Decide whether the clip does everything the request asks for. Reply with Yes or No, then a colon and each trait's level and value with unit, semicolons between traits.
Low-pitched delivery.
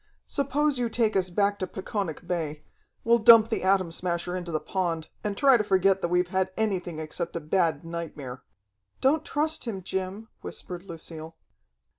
No: medium, 185 Hz